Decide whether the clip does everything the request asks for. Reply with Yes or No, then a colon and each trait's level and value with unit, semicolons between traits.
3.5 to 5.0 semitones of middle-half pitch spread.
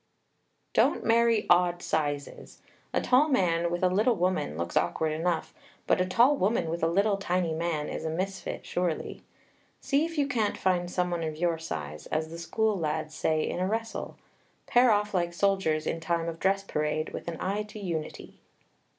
Yes: average, 4.3 semitones